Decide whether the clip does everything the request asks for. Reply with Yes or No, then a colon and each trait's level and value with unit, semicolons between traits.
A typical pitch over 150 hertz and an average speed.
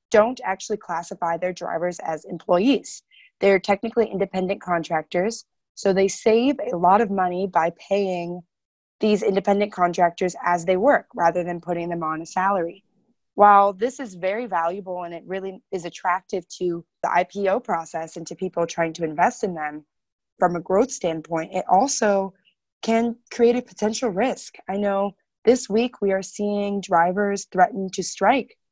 Yes: high, 190 Hz; average, 160 wpm